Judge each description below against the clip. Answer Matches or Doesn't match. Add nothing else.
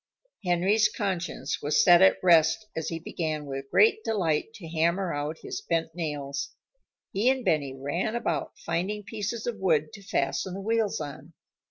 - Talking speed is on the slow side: Doesn't match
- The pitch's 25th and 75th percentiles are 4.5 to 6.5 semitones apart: Matches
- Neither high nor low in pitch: Matches